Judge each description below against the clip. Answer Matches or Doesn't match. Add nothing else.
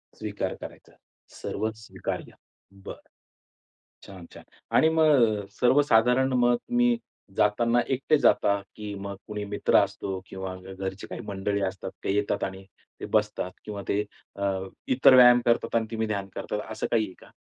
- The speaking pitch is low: Matches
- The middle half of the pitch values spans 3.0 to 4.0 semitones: Matches